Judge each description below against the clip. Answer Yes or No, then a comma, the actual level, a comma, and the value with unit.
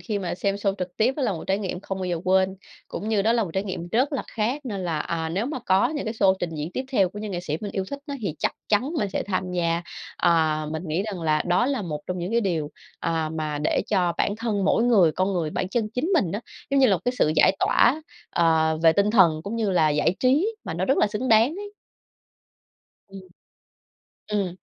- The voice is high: Yes, high, 195 Hz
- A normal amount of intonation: Yes, average, 4.7 semitones